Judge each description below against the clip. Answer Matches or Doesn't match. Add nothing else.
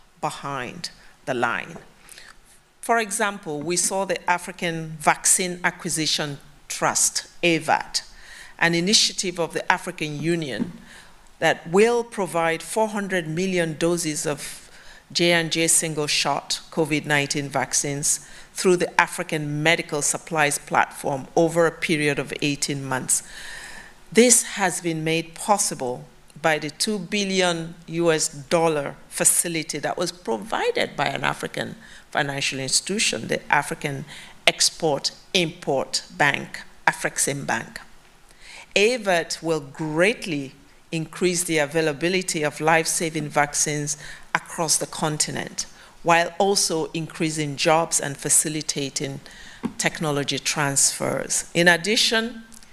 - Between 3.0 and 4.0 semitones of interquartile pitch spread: Matches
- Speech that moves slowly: Matches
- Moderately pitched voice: Matches